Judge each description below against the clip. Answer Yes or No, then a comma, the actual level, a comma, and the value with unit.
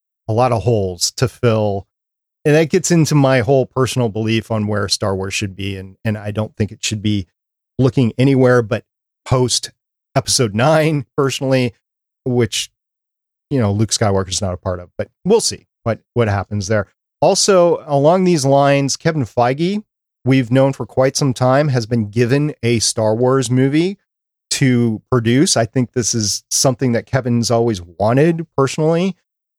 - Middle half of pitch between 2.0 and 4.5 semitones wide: Yes, average, 4.1 semitones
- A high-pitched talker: No, low, 125 Hz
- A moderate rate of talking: Yes, average, 170 wpm